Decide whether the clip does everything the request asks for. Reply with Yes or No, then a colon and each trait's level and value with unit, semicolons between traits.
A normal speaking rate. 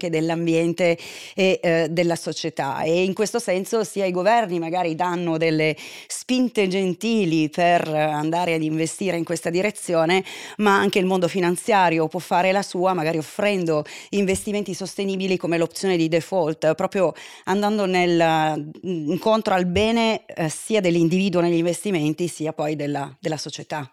Yes: average, 145 wpm